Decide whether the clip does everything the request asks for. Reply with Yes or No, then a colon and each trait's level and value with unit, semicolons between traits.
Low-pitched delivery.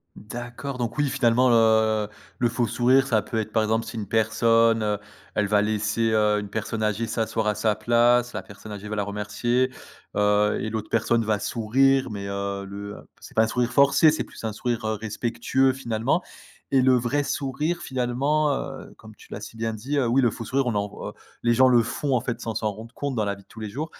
Yes: low, 115 Hz